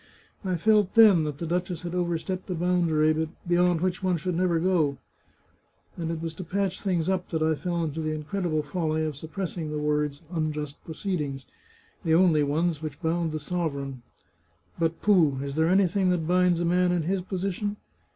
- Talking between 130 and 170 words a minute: No, average, 185 wpm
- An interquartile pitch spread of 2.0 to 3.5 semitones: Yes, average, 2.7 semitones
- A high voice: No, medium, 170 Hz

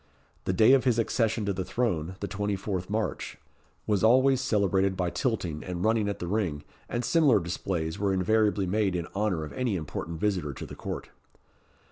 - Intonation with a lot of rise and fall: No, average, 3.6 semitones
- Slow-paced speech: No, average, 180 wpm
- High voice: No, low, 100 Hz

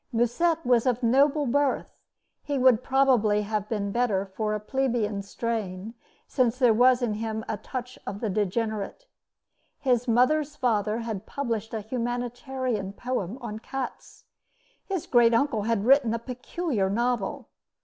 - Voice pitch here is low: No, high, 235 Hz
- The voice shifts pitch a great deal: No, average, 3.2 semitones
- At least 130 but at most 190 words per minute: Yes, average, 145 wpm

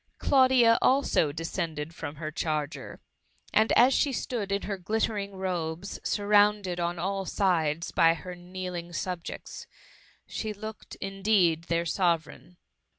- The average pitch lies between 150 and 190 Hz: Yes, medium, 185 Hz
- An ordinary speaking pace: No, slow, 125 wpm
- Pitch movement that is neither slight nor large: Yes, average, 3.6 semitones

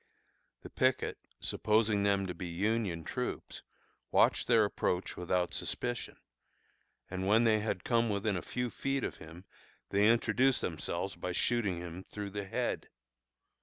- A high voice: No, low, 100 Hz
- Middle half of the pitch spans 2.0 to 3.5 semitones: No, average, 4.0 semitones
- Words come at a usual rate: Yes, average, 145 wpm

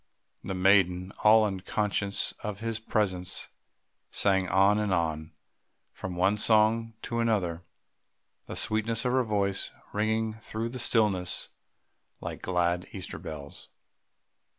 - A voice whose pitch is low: Yes, low, 100 Hz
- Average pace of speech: No, slow, 120 wpm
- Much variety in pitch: No, average, 3.2 semitones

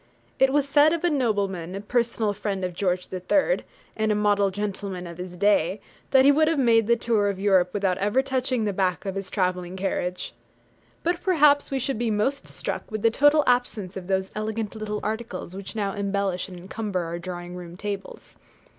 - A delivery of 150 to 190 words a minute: No, average, 200 wpm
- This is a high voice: Yes, high, 205 Hz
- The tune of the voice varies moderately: Yes, average, 4.1 semitones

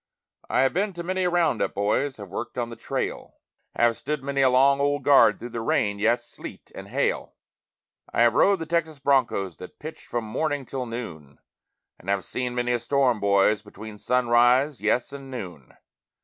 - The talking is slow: No, average, 190 wpm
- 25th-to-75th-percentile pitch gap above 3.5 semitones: Yes, average, 4.5 semitones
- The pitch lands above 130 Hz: No, low, 125 Hz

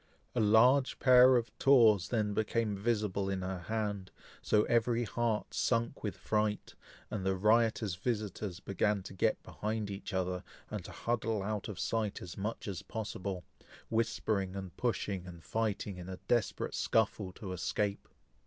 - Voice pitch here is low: Yes, low, 105 Hz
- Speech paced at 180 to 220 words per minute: No, average, 155 wpm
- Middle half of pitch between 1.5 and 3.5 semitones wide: Yes, average, 2.8 semitones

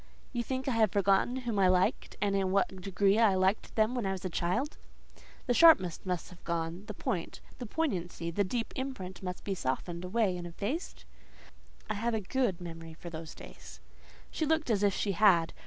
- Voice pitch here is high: Yes, high, 195 Hz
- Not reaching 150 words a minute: No, average, 185 wpm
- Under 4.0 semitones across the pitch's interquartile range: No, average, 4.5 semitones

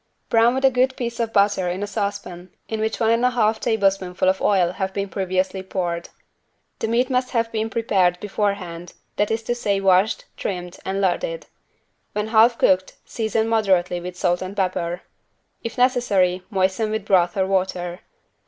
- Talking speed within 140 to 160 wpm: No, average, 175 wpm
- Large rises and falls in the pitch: No, average, 3.4 semitones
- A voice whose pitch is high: Yes, high, 200 Hz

